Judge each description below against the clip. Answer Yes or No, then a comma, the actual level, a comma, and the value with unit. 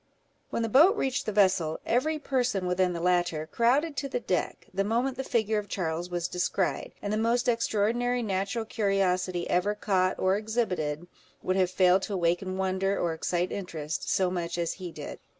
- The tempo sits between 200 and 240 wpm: No, average, 185 wpm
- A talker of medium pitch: No, high, 195 Hz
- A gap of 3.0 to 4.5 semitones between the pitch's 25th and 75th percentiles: Yes, average, 4.2 semitones